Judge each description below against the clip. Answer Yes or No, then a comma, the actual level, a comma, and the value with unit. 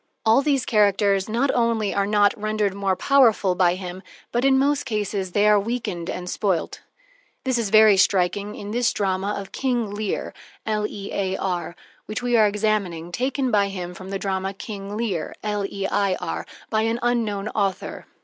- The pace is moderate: Yes, average, 155 wpm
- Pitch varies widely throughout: No, average, 2.8 semitones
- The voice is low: No, high, 205 Hz